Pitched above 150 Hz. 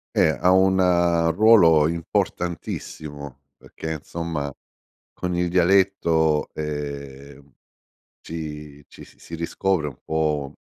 No: very low, 80 Hz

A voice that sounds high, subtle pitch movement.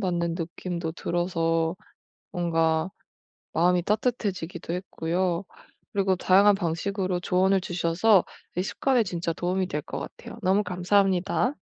No: medium, 180 Hz; narrow, 2.2 semitones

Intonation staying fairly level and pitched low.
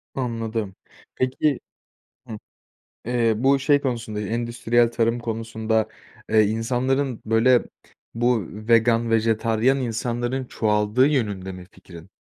Yes: narrow, 2.1 semitones; low, 115 Hz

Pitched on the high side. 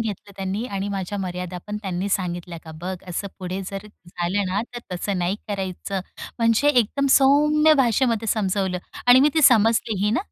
Yes: high, 200 Hz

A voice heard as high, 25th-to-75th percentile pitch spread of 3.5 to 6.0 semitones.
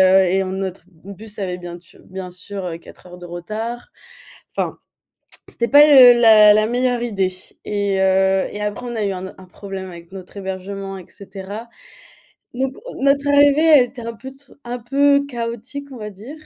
Yes: high, 210 Hz; average, 4.4 semitones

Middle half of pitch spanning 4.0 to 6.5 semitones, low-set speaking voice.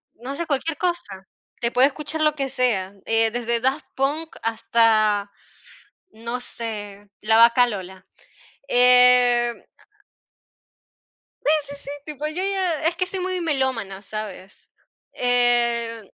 No: average, 4.6 semitones; high, 245 Hz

